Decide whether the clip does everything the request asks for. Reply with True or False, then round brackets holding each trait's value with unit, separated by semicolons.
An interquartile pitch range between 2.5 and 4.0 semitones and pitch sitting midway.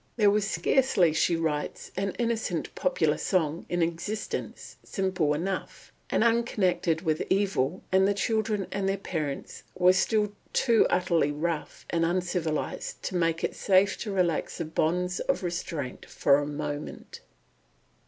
True (3.5 semitones; 180 Hz)